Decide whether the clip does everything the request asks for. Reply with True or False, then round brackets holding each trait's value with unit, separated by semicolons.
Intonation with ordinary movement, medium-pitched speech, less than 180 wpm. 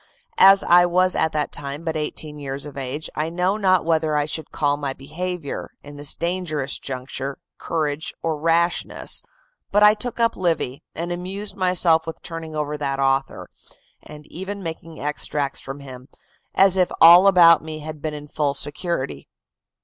True (3.5 semitones; 160 Hz; 170 wpm)